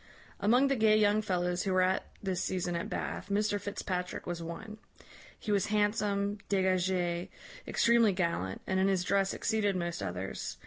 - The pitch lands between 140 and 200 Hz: Yes, high, 190 Hz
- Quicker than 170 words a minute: No, average, 165 wpm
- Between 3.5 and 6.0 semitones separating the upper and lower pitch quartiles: No, average, 2.7 semitones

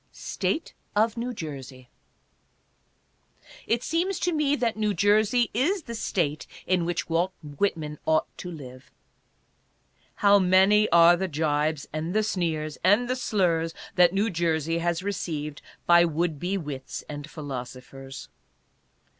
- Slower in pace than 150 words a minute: Yes, slow, 135 wpm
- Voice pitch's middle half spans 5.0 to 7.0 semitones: Yes, wide, 5.4 semitones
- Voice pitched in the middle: Yes, medium, 175 Hz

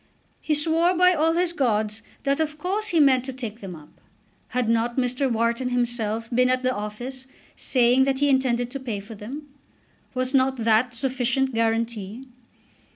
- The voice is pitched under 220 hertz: No, very high, 250 Hz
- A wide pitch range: No, average, 3.1 semitones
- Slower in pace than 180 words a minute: Yes, average, 170 wpm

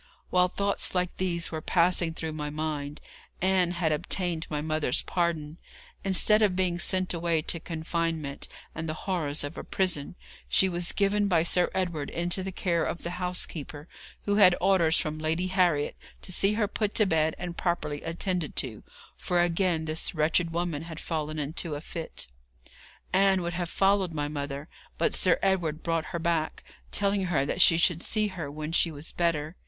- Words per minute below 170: No, average, 180 wpm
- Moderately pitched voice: Yes, medium, 170 Hz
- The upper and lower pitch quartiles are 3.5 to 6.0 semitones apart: No, average, 2.8 semitones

